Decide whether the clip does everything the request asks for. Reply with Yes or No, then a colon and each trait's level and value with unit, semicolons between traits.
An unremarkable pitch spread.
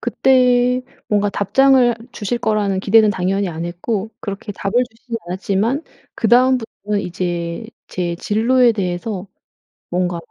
Yes: average, 4.4 semitones